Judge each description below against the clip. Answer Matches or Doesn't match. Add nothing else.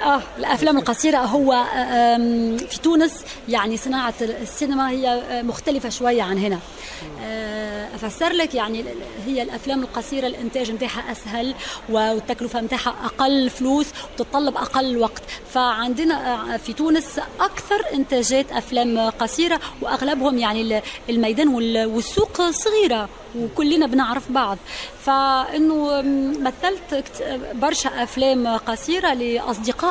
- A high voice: Matches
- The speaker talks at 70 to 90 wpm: Doesn't match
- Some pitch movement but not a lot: Matches